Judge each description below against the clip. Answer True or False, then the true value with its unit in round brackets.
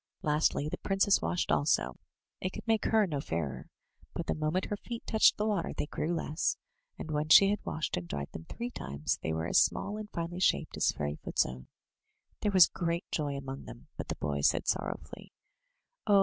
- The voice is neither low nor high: True (160 Hz)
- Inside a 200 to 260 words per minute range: True (205 wpm)